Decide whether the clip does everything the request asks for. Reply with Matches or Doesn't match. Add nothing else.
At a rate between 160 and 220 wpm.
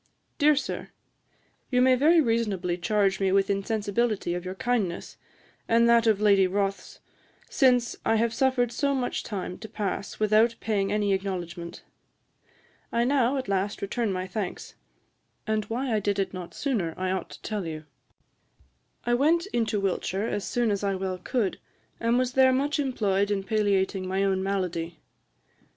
Matches